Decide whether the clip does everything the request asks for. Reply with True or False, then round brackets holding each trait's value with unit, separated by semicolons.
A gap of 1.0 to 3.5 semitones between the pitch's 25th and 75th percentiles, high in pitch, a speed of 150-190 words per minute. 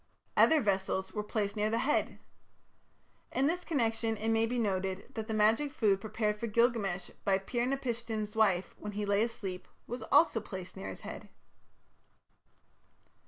True (2.8 semitones; 215 Hz; 160 wpm)